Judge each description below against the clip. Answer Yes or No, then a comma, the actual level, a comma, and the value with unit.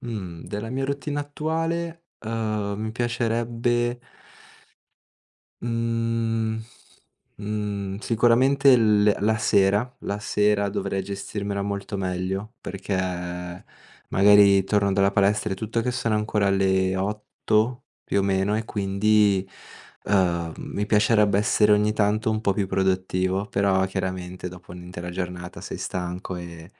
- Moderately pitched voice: No, low, 105 Hz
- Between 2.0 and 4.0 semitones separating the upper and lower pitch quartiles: Yes, average, 2.7 semitones